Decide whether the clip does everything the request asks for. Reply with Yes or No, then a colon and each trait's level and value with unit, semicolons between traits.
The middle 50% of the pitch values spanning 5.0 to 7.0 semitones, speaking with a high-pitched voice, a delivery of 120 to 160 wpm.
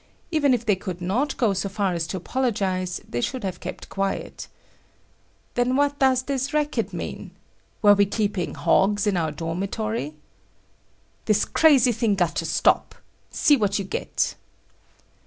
Yes: wide, 5.5 semitones; high, 205 Hz; average, 155 wpm